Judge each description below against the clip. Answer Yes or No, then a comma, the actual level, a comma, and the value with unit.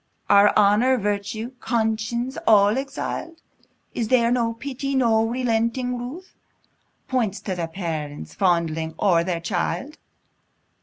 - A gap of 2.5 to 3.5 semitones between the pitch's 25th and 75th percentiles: No, average, 4.2 semitones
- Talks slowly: Yes, slow, 115 wpm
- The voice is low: No, high, 225 Hz